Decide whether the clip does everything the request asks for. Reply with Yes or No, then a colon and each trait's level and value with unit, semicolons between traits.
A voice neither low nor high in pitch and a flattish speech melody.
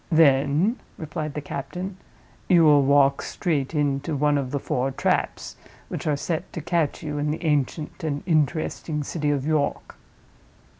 Yes: medium, 150 Hz; narrow, 2.3 semitones